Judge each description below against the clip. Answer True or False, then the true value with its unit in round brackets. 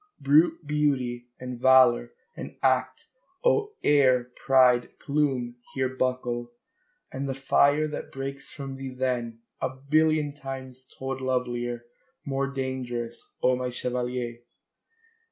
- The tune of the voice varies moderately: False (1.9 semitones)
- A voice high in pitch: False (130 Hz)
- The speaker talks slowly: True (120 wpm)